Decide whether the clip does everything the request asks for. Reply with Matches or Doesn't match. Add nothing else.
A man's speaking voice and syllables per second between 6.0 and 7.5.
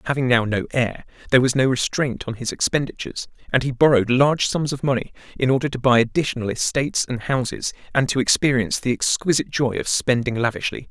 Matches